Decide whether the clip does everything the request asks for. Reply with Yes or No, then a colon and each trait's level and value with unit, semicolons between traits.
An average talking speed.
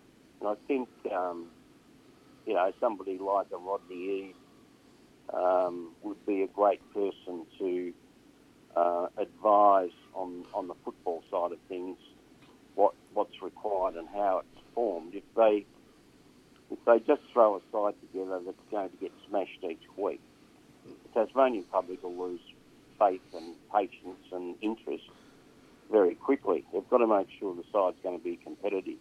Yes: average, 155 wpm